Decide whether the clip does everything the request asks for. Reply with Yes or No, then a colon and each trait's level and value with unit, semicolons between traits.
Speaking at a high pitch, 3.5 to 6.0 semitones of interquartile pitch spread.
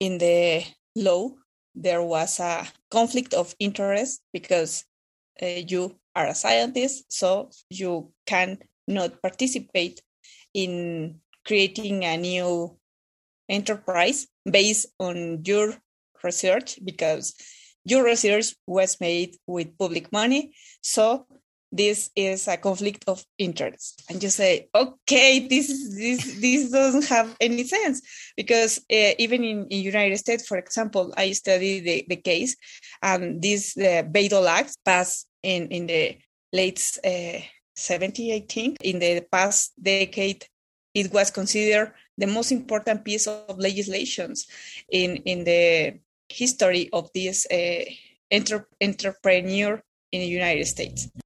Yes: high, 195 Hz; average, 4.3 semitones